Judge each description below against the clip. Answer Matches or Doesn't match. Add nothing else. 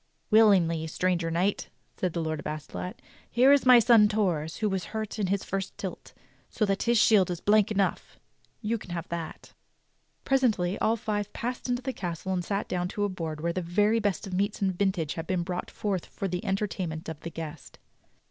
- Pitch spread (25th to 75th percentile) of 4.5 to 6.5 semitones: Doesn't match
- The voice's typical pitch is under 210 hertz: Matches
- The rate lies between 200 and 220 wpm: Matches